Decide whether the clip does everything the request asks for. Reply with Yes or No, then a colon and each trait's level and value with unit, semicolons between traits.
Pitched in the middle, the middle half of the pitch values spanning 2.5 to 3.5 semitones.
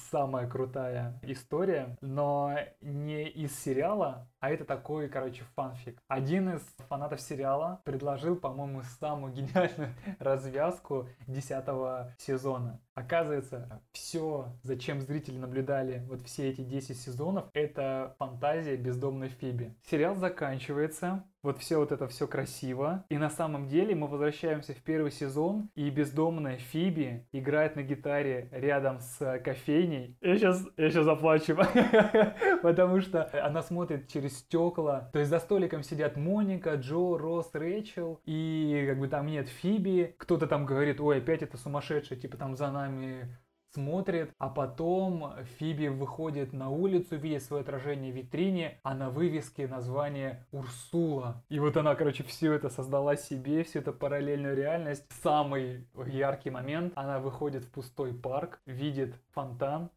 Yes: medium, 145 Hz; average, 3.1 semitones